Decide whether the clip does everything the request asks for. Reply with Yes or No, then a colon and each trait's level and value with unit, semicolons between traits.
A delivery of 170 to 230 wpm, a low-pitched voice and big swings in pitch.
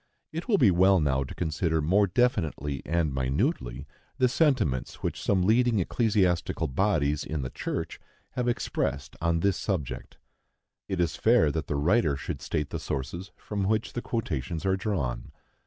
No: average, 160 wpm; very low, 85 Hz; wide, 6.6 semitones